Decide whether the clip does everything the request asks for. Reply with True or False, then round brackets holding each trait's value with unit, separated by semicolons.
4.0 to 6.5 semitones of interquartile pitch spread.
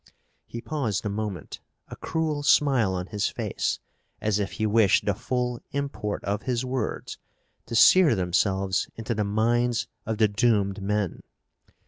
False (3.3 semitones)